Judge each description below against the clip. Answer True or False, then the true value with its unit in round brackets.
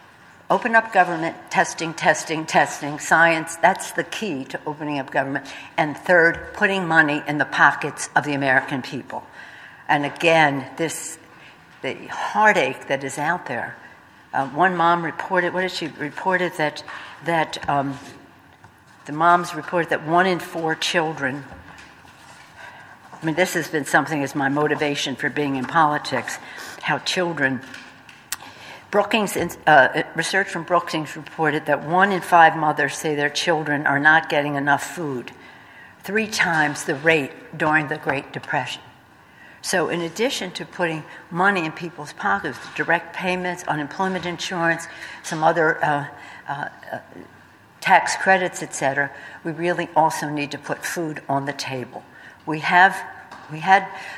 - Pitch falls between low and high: True (160 Hz)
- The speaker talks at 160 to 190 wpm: False (140 wpm)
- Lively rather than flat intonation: False (3.0 semitones)